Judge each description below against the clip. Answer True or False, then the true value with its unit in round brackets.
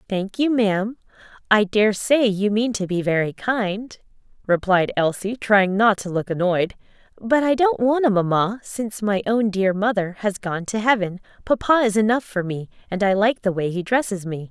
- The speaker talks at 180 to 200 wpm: True (190 wpm)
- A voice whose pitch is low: False (210 Hz)